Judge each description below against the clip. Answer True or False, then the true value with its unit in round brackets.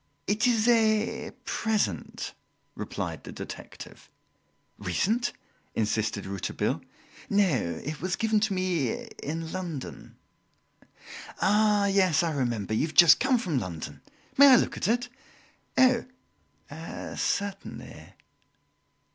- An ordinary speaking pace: False (110 wpm)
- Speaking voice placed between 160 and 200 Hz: True (190 Hz)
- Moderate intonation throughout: False (7.1 semitones)